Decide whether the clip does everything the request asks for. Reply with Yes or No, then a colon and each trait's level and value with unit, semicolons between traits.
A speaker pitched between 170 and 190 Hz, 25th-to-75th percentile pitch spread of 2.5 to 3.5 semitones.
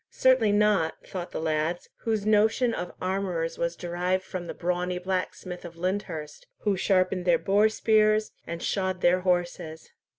Yes: medium, 185 Hz; average, 2.8 semitones